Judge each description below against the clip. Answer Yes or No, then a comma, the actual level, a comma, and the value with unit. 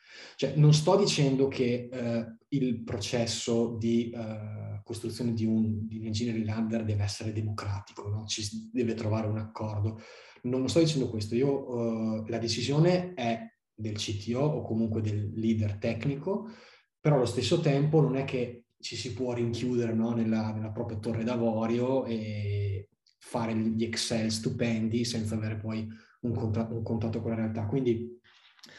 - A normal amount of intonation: No, narrow, 1.9 semitones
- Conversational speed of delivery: Yes, average, 155 wpm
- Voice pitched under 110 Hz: No, low, 115 Hz